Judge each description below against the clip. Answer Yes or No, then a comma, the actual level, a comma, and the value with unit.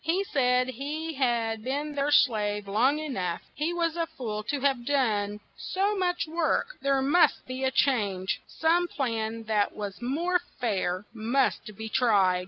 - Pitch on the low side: No, very high, 260 Hz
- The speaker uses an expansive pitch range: Yes, wide, 5.8 semitones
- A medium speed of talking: Yes, average, 165 wpm